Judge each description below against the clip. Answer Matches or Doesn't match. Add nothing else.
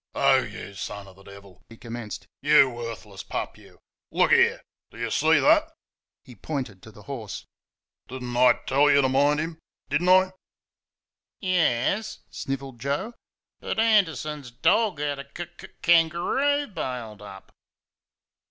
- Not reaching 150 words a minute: Doesn't match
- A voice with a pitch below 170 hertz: Matches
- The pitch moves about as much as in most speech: Doesn't match